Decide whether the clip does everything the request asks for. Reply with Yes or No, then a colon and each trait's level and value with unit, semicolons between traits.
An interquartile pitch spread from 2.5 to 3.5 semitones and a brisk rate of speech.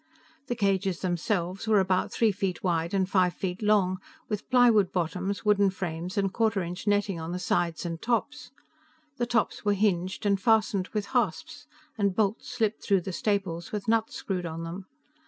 No: average, 2.9 semitones; average, 175 wpm